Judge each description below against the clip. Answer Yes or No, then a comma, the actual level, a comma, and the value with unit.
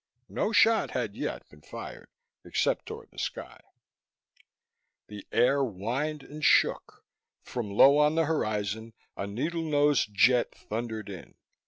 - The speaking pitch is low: Yes, low, 125 Hz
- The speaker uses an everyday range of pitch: No, wide, 6.1 semitones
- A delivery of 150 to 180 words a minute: No, slow, 135 wpm